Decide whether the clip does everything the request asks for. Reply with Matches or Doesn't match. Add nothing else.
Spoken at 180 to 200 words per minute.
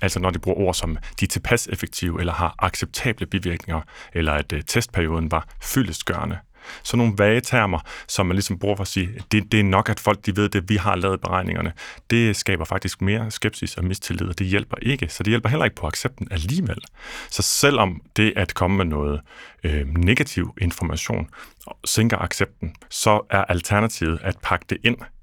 Matches